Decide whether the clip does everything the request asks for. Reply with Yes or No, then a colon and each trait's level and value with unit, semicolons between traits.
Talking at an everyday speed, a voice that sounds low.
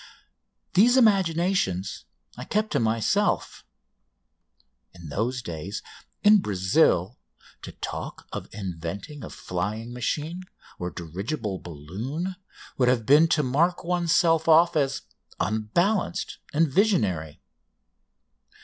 No: slow, 105 wpm; low, 130 Hz